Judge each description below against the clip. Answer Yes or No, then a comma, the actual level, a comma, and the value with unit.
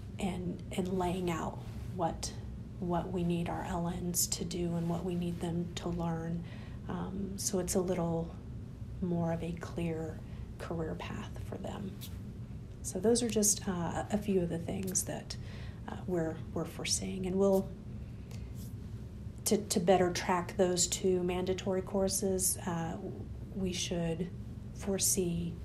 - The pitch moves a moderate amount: No, wide, 7.9 semitones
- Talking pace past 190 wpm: No, average, 145 wpm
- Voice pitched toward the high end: No, medium, 175 Hz